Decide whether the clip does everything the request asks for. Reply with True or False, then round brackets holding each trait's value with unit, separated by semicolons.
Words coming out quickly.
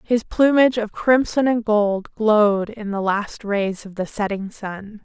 False (180 wpm)